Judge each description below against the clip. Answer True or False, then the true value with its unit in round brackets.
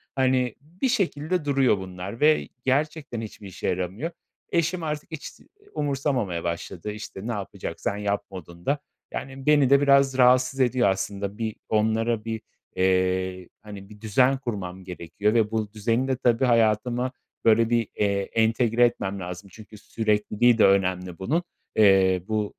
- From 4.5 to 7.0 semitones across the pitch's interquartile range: True (5.0 semitones)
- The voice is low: True (110 Hz)